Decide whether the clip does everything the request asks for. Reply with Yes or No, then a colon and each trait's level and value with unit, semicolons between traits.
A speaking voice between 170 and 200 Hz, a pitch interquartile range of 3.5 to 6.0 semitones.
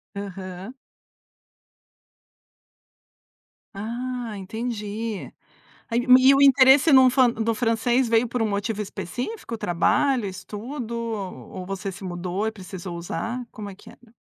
No: high, 225 Hz; average, 3.9 semitones